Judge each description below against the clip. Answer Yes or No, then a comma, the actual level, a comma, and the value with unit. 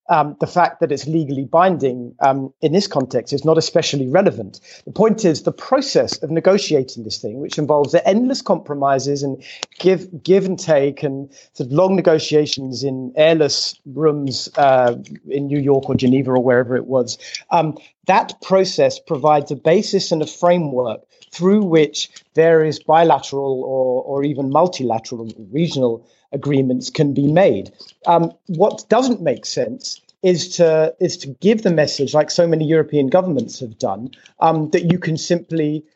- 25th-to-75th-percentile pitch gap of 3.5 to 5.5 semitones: Yes, average, 4.1 semitones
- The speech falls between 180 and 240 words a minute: No, average, 165 wpm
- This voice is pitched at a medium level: Yes, medium, 150 Hz